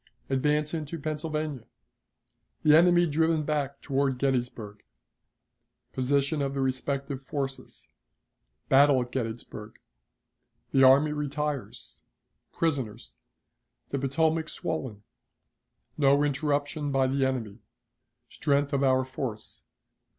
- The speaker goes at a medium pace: No, slow, 100 wpm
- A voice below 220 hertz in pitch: Yes, medium, 140 Hz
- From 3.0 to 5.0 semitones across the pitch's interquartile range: No, narrow, 2.4 semitones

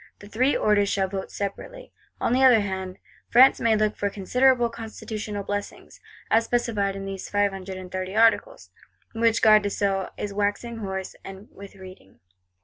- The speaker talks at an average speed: Yes, average, 160 wpm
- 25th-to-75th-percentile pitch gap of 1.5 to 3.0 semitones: Yes, average, 2.7 semitones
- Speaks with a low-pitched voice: No, high, 205 Hz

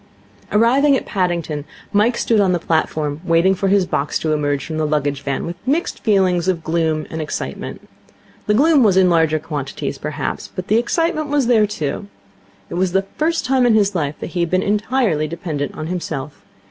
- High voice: No, medium, 180 Hz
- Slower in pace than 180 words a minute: No, average, 200 wpm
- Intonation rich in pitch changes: Yes, wide, 5.7 semitones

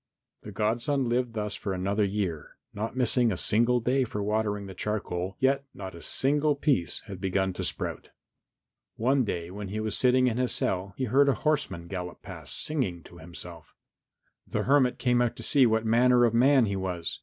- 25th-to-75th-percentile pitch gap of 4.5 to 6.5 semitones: Yes, average, 4.8 semitones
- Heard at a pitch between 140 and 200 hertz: No, low, 110 Hz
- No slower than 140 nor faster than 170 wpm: No, average, 190 wpm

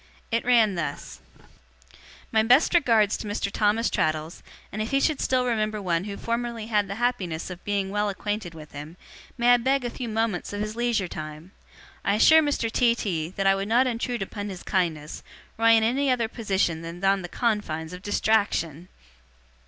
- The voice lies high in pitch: Yes, high, 210 Hz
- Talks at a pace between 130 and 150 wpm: No, average, 190 wpm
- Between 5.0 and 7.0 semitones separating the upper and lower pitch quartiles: No, average, 4.3 semitones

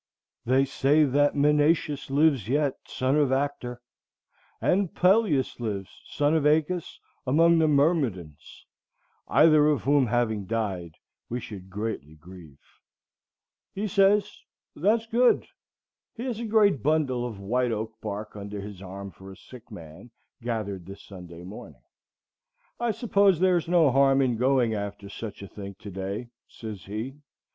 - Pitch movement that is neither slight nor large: No, wide, 7.2 semitones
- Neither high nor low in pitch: No, low, 125 Hz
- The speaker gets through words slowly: No, average, 145 wpm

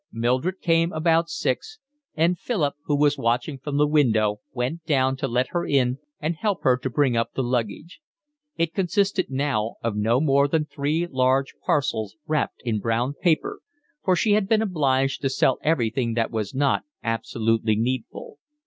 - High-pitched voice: No, low, 135 Hz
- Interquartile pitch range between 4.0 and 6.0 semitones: Yes, wide, 5.4 semitones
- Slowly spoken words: No, average, 170 wpm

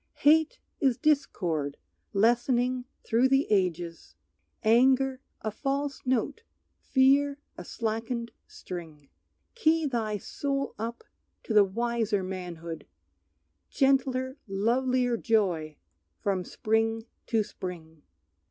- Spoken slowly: Yes, slow, 95 wpm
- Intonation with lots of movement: Yes, wide, 5.7 semitones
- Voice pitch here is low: No, high, 230 Hz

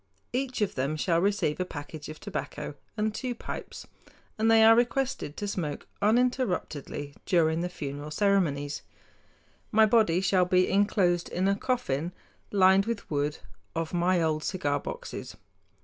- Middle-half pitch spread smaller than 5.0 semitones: No, wide, 5.6 semitones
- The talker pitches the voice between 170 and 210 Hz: Yes, medium, 185 Hz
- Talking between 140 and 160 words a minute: Yes, average, 150 wpm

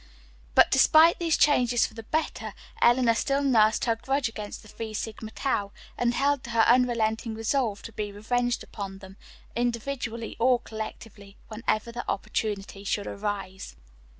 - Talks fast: No, average, 150 wpm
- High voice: Yes, high, 230 Hz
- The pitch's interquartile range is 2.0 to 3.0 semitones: Yes, narrow, 2.5 semitones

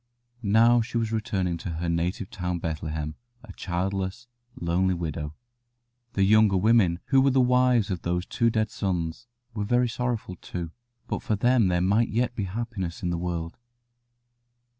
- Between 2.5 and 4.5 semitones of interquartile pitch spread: No, average, 4.9 semitones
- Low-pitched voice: Yes, very low, 95 Hz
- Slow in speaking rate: No, average, 165 wpm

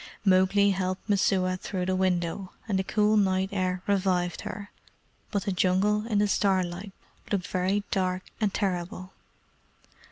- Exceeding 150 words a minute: No, average, 140 wpm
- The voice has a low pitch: No, high, 190 Hz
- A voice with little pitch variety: Yes, narrow, 1.6 semitones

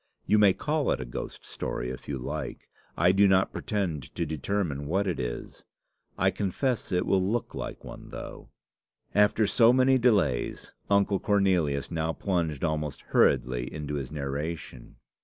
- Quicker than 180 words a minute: No, average, 155 wpm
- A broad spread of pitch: Yes, wide, 5.9 semitones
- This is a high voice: No, very low, 90 Hz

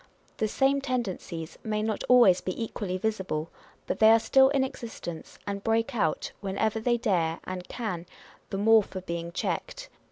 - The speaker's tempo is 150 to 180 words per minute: Yes, average, 165 wpm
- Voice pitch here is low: No, high, 215 Hz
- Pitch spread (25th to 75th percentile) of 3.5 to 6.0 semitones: Yes, average, 4.0 semitones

